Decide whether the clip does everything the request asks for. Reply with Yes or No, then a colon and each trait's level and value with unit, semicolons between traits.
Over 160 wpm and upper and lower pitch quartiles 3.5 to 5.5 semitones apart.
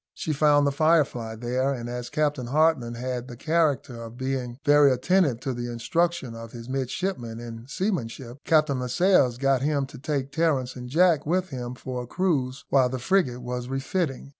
Yes: average, 180 wpm; average, 3.8 semitones